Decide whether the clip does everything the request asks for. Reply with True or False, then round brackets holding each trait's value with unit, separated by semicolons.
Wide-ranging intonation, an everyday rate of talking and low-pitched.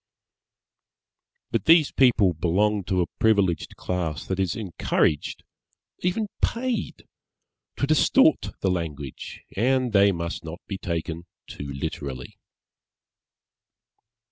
False (6.4 semitones; 110 wpm; 95 Hz)